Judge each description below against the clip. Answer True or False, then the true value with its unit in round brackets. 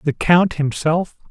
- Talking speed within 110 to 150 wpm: True (140 wpm)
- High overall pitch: False (160 Hz)